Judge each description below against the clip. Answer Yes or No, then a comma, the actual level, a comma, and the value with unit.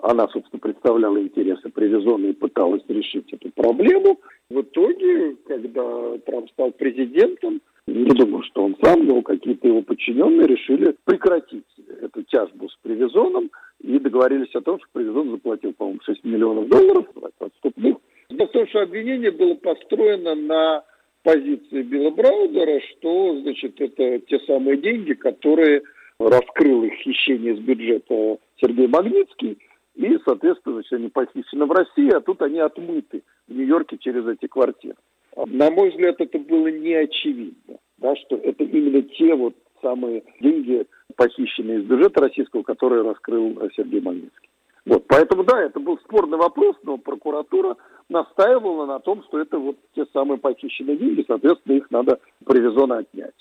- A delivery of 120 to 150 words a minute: Yes, average, 145 wpm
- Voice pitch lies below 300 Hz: No, very high, 315 Hz